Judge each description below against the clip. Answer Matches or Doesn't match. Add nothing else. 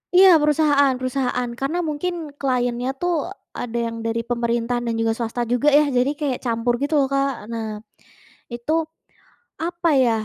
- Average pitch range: Matches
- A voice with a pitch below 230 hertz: Doesn't match